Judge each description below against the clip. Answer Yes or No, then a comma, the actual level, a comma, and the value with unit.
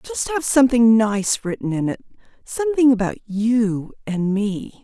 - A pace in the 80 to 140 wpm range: Yes, slow, 135 wpm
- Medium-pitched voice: No, high, 230 Hz